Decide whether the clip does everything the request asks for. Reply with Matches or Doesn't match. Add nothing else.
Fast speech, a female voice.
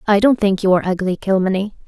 Matches